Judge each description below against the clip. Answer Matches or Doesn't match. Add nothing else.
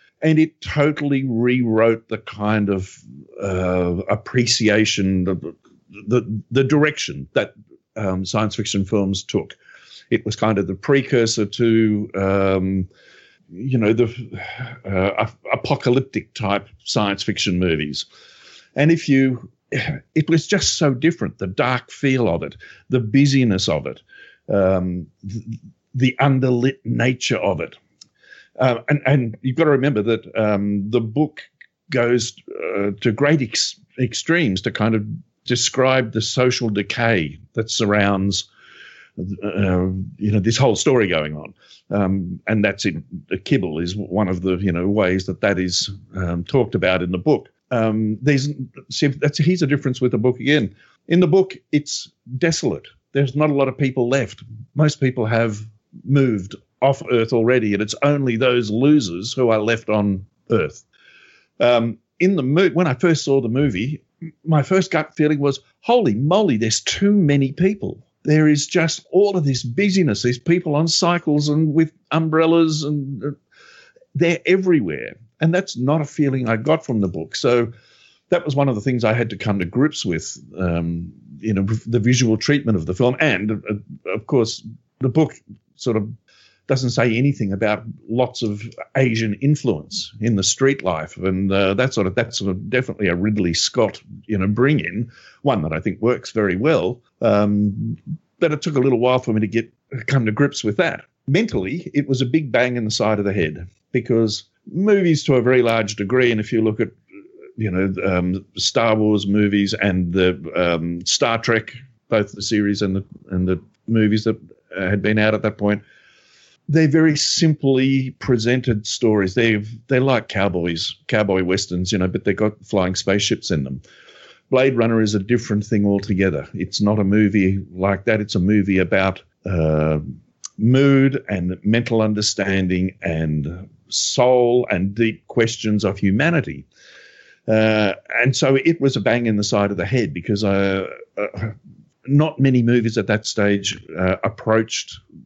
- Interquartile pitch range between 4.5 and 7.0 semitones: Matches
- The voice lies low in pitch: Matches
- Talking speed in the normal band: Matches